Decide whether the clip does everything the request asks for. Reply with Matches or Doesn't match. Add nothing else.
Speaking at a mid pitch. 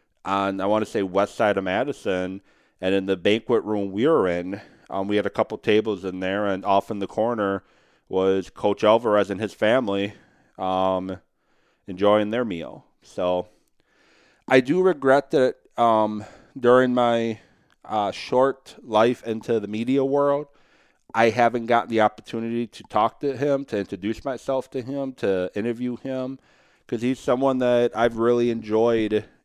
Doesn't match